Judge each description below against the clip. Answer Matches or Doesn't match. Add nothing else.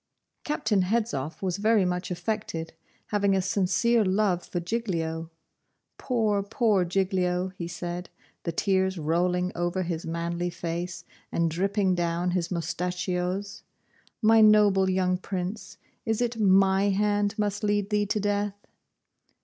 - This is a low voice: Doesn't match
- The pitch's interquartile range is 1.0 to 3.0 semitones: Matches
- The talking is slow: Matches